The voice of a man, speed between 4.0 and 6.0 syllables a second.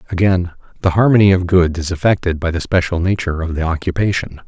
No: male; 6.4 syllables/s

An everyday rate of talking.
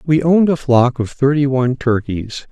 Yes: average, 190 wpm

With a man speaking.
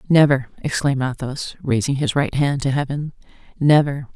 No: female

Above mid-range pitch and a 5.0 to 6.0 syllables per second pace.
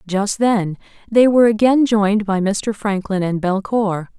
No: high, 205 Hz; 4.4 syllables/s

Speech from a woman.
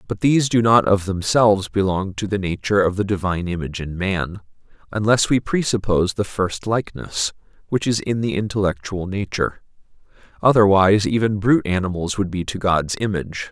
No: male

